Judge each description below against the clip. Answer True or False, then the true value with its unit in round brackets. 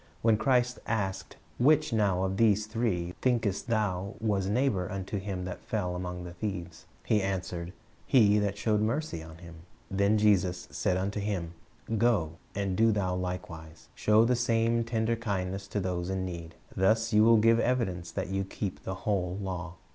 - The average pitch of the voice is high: False (100 Hz)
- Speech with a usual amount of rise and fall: True (3.5 semitones)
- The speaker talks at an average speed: True (170 wpm)